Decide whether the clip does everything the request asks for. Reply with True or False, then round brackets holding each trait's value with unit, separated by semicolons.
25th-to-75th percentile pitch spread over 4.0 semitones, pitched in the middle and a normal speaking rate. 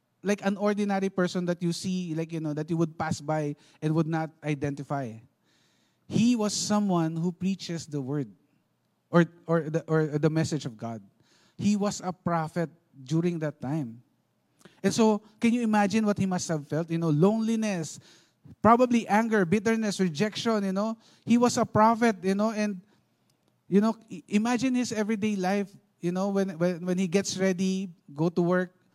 True (4.5 semitones; 180 Hz; 175 wpm)